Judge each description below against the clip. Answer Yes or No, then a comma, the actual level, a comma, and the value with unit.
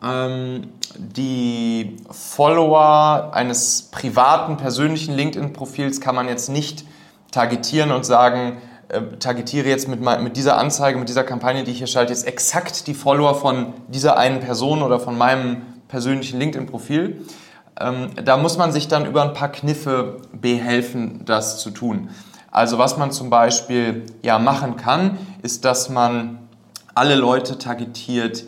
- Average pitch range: Yes, average, 3.0 semitones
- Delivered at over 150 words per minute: No, average, 145 wpm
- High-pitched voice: No, low, 130 Hz